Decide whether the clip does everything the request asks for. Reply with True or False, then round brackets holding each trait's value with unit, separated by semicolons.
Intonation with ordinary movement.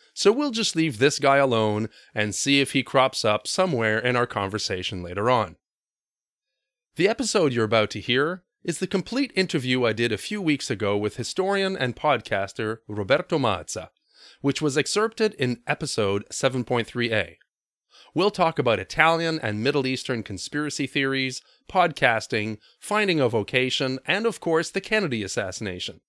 False (6.8 semitones)